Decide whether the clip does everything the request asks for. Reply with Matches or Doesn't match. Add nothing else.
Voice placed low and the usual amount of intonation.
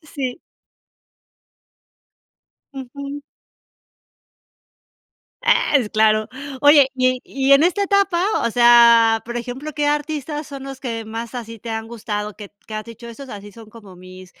Doesn't match